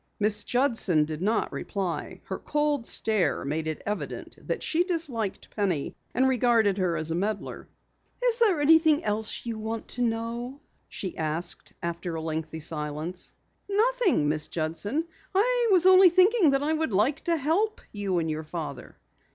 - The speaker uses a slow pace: No, average, 160 wpm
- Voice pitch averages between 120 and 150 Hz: No, high, 220 Hz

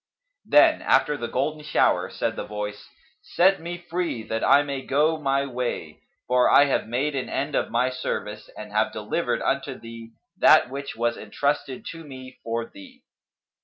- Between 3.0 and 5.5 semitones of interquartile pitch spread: Yes, average, 4.4 semitones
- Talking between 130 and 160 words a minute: No, average, 170 wpm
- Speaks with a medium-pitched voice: No, low, 130 Hz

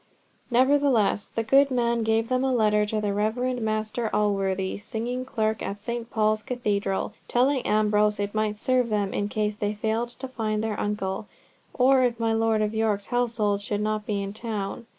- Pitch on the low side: No, high, 215 Hz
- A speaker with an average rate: Yes, average, 180 wpm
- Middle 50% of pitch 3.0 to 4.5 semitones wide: No, narrow, 2.4 semitones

